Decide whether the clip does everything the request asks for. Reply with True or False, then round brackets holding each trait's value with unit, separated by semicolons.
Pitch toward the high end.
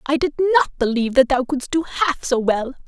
True (270 Hz)